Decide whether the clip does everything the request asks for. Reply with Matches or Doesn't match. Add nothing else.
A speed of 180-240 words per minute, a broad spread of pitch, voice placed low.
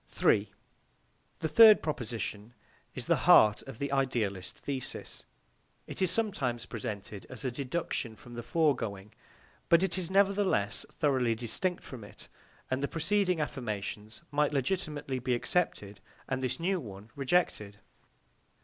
Doesn't match